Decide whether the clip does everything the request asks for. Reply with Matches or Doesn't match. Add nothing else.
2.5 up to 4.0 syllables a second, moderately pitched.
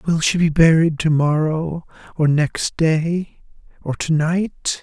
Matches